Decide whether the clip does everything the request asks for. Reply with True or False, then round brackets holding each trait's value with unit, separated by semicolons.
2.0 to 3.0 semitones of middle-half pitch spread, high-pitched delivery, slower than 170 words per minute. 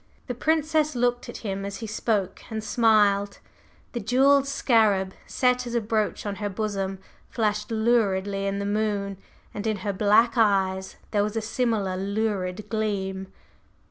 True (2.6 semitones; 210 Hz; 155 wpm)